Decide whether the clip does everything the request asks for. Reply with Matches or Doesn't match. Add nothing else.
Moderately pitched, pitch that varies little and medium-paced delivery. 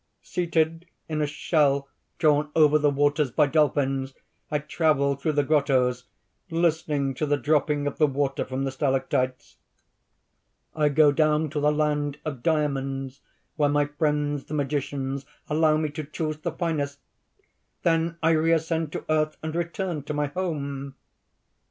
Matches